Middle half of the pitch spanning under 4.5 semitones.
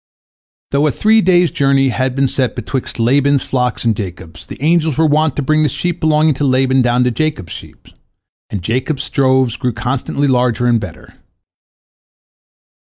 Yes: average, 3.5 semitones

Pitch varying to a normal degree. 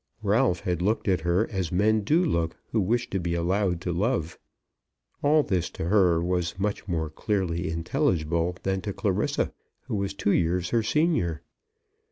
Yes: average, 3.8 semitones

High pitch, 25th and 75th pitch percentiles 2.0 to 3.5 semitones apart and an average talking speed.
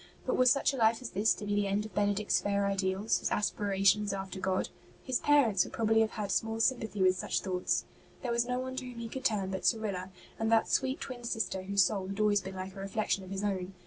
No: high, 205 Hz; average, 2.7 semitones; fast, 245 wpm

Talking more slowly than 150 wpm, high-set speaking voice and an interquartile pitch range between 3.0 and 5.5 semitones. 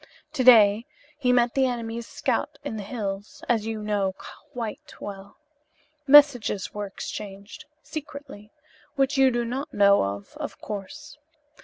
Yes: average, 140 wpm; high, 225 Hz; average, 4.5 semitones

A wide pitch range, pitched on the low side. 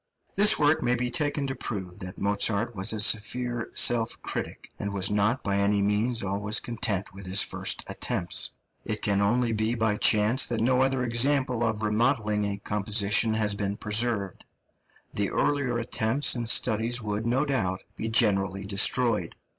No: average, 3.2 semitones; low, 110 Hz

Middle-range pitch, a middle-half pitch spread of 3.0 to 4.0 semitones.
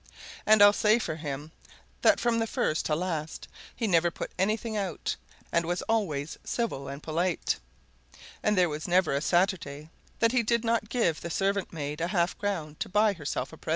No: medium, 180 Hz; average, 5.2 semitones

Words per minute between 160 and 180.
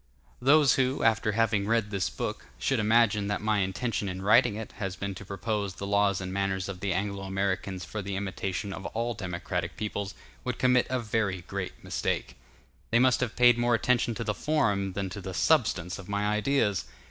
No: average, 195 wpm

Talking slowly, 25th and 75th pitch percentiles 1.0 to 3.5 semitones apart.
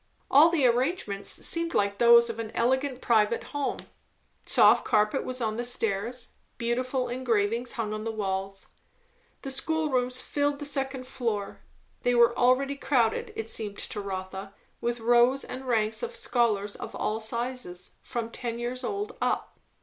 No: average, 155 wpm; average, 3.2 semitones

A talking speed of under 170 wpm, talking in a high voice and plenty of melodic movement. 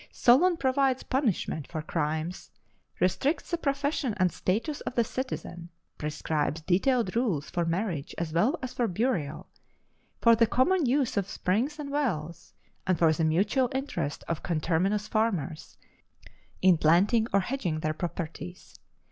Yes: average, 140 wpm; high, 195 Hz; wide, 7.7 semitones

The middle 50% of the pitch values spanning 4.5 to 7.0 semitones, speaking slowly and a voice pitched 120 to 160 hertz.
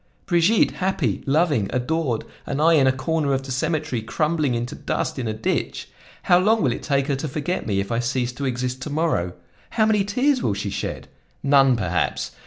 No: average, 5.1 semitones; average, 200 wpm; medium, 140 Hz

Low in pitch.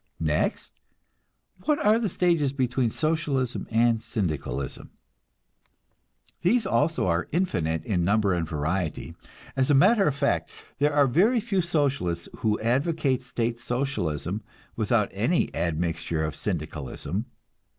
Yes: low, 125 Hz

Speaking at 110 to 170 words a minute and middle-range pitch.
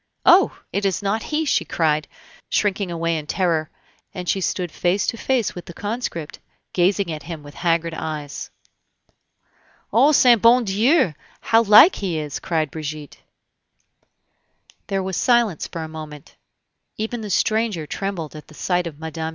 Yes: average, 160 wpm; medium, 180 Hz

